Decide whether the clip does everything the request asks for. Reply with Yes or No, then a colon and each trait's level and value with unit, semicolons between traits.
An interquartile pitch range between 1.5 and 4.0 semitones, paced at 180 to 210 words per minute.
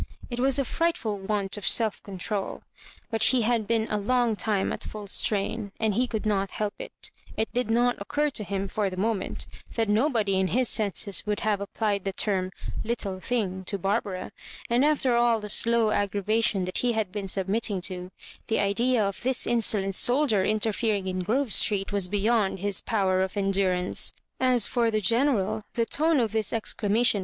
Yes: average, 3.0 semitones; average, 195 wpm